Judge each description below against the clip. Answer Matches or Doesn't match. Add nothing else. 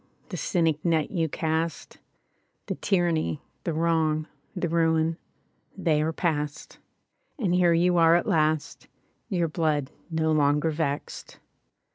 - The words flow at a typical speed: Doesn't match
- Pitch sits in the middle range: Matches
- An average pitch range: Doesn't match